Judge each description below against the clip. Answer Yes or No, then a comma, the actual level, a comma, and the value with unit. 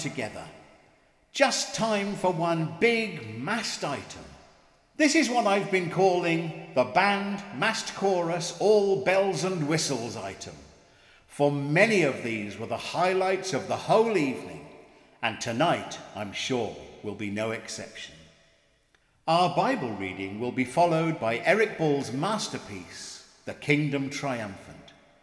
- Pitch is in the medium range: Yes, medium, 165 Hz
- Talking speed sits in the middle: No, slow, 130 wpm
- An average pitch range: No, wide, 8.7 semitones